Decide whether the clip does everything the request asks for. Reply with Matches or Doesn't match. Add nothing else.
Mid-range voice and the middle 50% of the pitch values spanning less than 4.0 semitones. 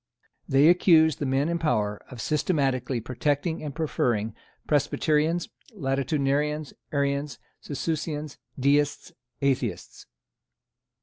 Matches